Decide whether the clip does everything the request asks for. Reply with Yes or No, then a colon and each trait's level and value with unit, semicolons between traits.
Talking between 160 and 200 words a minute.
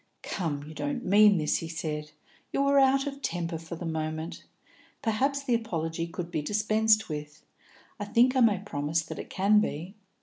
Yes: average, 180 wpm